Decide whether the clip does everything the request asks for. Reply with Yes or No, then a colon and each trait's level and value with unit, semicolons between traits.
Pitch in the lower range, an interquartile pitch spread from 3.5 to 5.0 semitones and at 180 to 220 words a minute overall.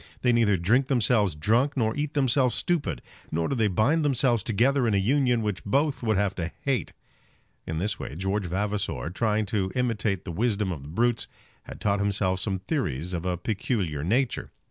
Yes: low, 105 Hz; average, 4.7 semitones; average, 190 wpm